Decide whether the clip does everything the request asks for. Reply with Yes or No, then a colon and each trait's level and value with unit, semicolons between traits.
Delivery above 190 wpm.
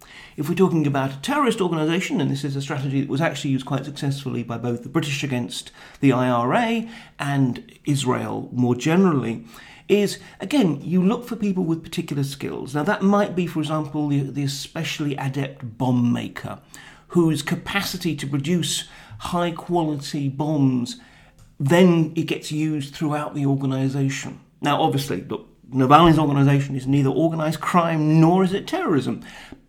No: average, 155 wpm